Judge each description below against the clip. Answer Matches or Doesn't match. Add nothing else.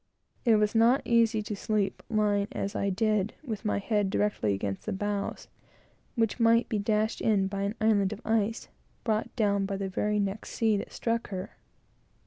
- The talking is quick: Doesn't match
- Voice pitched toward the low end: Doesn't match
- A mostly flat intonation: Matches